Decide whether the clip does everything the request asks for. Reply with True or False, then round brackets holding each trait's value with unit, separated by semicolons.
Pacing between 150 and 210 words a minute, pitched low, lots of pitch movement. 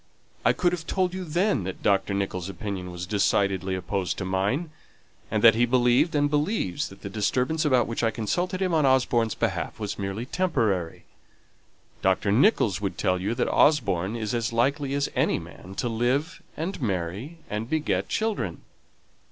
True (165 wpm; 115 Hz; 7.2 semitones)